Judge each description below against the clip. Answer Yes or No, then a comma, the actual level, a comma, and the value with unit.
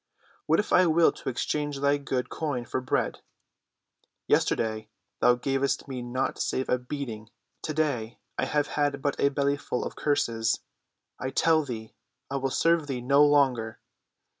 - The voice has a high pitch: No, medium, 140 Hz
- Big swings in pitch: No, average, 2.9 semitones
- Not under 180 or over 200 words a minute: No, average, 155 wpm